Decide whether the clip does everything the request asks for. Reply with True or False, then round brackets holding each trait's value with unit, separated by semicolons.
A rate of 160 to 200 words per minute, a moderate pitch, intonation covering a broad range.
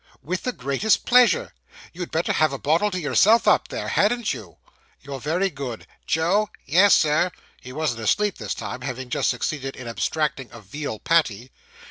True (170 wpm; 155 Hz; 6.2 semitones)